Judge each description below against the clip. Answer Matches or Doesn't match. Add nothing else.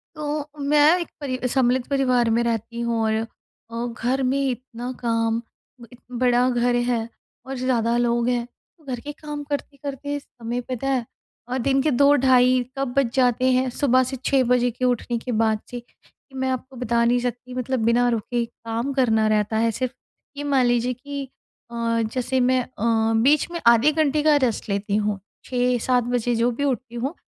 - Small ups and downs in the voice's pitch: Matches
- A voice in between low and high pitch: Doesn't match